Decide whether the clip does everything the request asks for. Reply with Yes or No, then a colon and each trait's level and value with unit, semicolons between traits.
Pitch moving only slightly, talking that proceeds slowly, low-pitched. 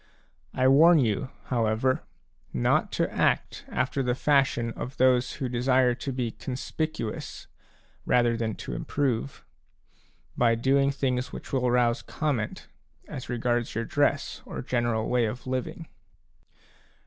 Yes: narrow, 2.3 semitones; slow, 130 wpm; low, 125 Hz